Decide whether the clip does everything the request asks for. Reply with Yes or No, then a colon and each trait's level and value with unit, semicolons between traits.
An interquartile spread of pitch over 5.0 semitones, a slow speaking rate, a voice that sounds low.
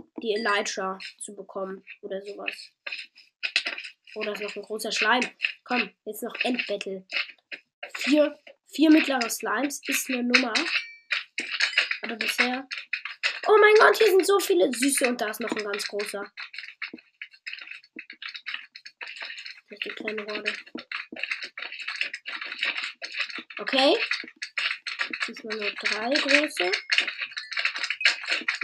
No: wide, 5.5 semitones; slow, 90 wpm; high, 240 Hz